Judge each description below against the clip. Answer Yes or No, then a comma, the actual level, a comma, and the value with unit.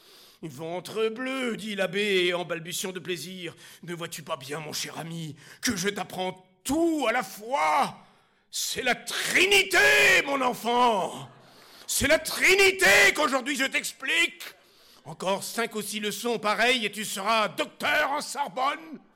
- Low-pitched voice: No, high, 215 Hz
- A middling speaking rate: No, slow, 140 wpm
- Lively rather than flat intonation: Yes, wide, 6.8 semitones